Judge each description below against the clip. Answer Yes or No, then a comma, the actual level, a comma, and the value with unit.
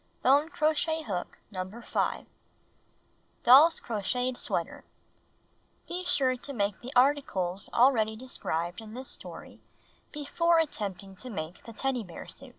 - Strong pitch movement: Yes, wide, 5.9 semitones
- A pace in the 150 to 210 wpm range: No, slow, 135 wpm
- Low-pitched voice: No, very high, 250 Hz